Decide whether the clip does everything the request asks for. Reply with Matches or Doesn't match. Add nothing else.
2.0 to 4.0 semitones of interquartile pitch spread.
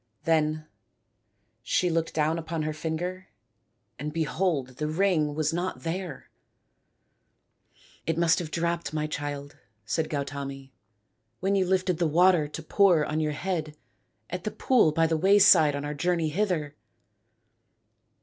Matches